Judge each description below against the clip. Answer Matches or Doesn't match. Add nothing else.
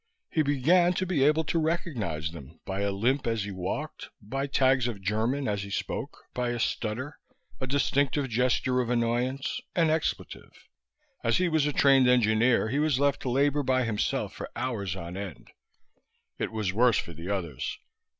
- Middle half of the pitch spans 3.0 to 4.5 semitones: Doesn't match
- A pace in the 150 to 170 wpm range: Doesn't match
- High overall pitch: Doesn't match